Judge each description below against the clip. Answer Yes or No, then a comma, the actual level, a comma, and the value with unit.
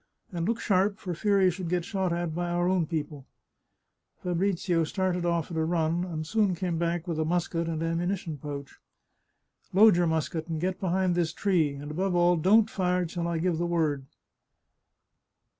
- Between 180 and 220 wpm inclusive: Yes, average, 190 wpm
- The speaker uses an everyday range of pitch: No, narrow, 2.3 semitones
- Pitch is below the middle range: No, medium, 175 Hz